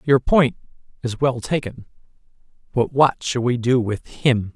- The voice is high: No, low, 125 Hz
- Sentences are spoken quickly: No, average, 160 wpm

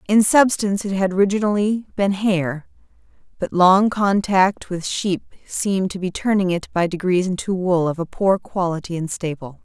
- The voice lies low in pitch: No, high, 190 Hz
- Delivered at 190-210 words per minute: No, average, 170 wpm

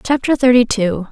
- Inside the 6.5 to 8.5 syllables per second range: No, 5.0 syllables/s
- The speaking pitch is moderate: No, high, 240 Hz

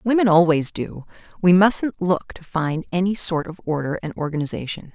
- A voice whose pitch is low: No, medium, 175 Hz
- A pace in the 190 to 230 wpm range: No, average, 170 wpm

